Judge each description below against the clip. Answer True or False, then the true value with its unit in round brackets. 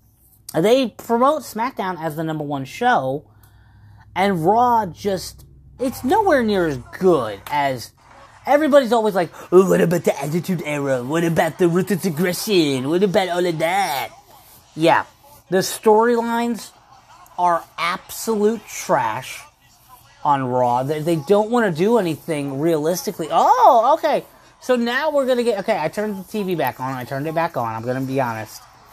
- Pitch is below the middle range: False (175 Hz)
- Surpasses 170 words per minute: False (155 wpm)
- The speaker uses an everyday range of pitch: False (7.8 semitones)